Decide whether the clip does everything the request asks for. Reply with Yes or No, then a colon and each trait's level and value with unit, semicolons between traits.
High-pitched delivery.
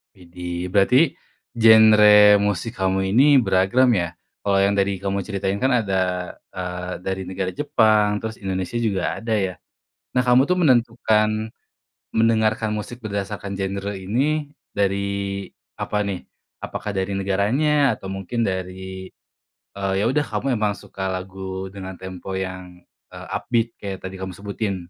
No: low, 100 Hz